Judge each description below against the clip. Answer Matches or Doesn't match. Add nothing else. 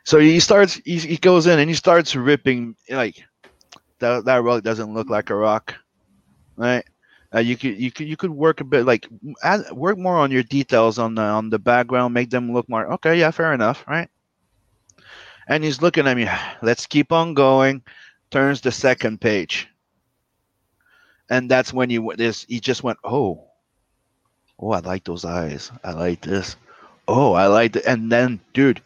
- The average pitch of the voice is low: Matches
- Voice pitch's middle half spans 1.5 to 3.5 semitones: Doesn't match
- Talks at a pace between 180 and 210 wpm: Matches